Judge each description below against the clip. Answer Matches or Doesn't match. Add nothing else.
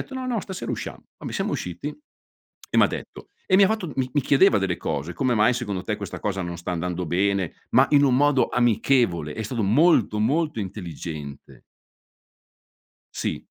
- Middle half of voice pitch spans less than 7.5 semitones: Doesn't match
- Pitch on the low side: Matches